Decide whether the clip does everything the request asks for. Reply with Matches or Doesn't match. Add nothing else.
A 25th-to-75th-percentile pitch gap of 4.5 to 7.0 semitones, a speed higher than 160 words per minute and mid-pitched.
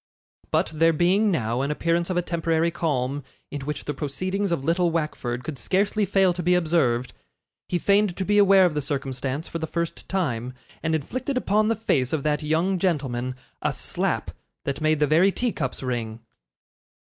Matches